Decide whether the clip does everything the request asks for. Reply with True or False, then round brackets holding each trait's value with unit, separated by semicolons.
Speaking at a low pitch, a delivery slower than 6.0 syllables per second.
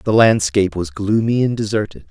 True (105 Hz; 5.4 syllables/s)